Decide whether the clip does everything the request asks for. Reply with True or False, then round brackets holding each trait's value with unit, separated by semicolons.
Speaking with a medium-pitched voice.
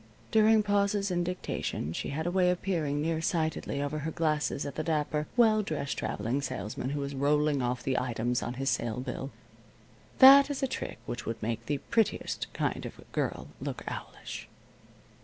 True (150 Hz)